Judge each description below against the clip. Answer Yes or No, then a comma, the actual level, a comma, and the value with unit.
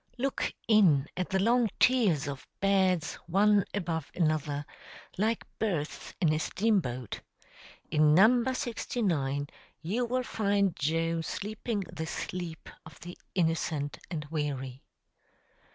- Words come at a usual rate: No, slow, 125 wpm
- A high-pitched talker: No, medium, 175 Hz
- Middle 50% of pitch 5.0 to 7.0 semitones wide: Yes, wide, 5.6 semitones